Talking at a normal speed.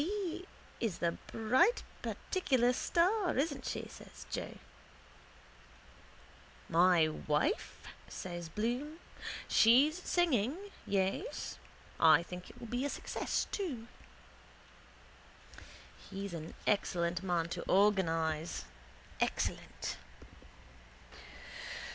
No: slow, 90 wpm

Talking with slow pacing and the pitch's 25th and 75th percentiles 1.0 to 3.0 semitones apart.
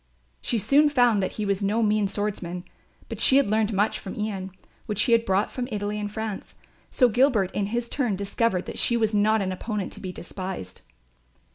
No: fast, 205 wpm; average, 2.7 semitones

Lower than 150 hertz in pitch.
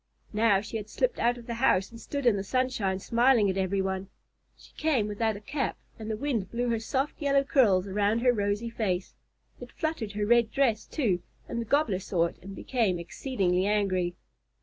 No: high, 220 Hz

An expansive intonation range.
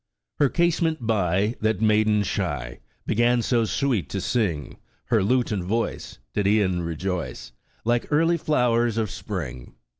No: average, 4.8 semitones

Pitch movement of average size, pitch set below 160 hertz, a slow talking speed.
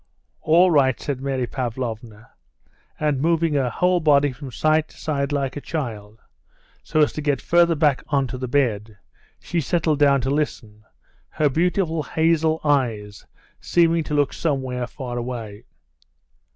No: average, 4.0 semitones; medium, 140 Hz; average, 150 wpm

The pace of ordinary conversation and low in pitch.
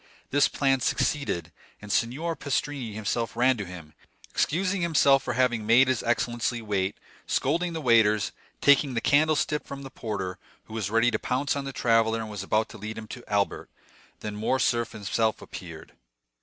Yes: average, 170 wpm; low, 115 Hz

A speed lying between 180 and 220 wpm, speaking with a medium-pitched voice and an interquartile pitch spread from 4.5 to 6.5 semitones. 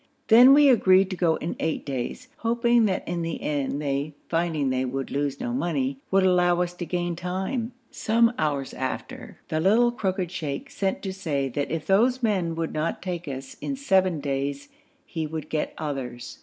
Yes: average, 185 wpm; medium, 170 Hz; average, 5.2 semitones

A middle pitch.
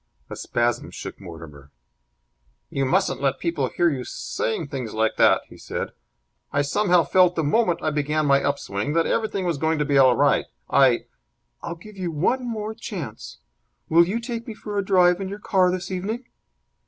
Yes: medium, 165 Hz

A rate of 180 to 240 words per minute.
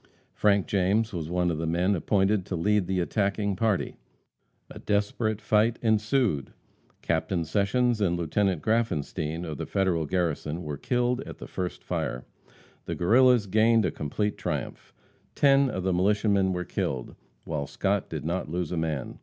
No: average, 160 wpm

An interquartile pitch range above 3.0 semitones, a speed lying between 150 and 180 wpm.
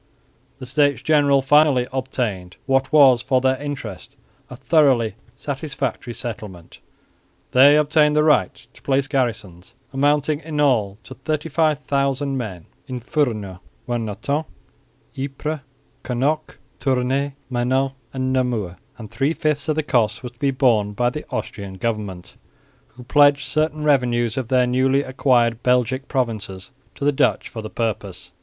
No: average, 3.4 semitones; average, 140 wpm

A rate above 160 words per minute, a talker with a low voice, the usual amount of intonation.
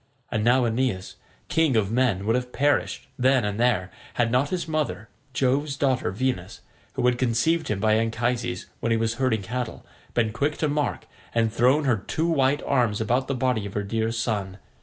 Yes: average, 190 wpm; low, 120 Hz; average, 3.1 semitones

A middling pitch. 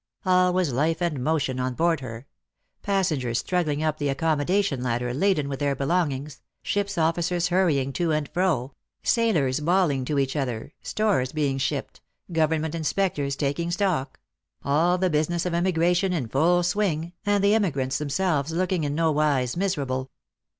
Yes: medium, 155 Hz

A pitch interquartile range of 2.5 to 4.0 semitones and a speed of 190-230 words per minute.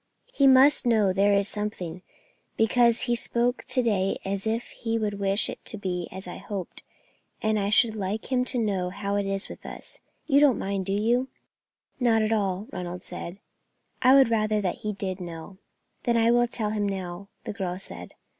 Yes: average, 3.3 semitones; average, 200 wpm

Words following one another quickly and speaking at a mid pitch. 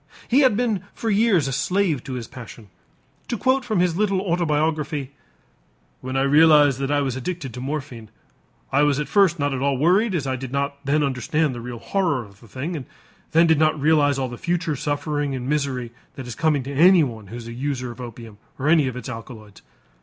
Yes: fast, 215 wpm; medium, 145 Hz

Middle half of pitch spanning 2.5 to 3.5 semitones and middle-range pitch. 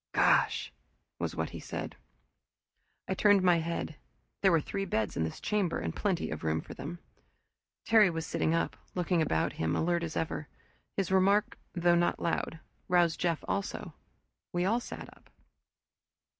Yes: average, 2.9 semitones; medium, 175 Hz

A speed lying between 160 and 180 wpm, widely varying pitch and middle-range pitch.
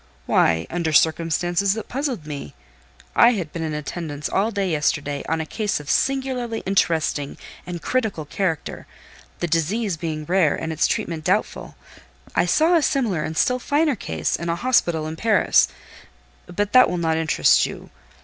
Yes: average, 165 wpm; wide, 6.0 semitones; medium, 170 Hz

